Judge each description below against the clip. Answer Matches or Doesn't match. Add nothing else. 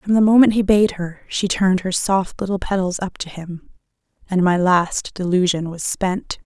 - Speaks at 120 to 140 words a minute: Doesn't match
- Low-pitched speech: Doesn't match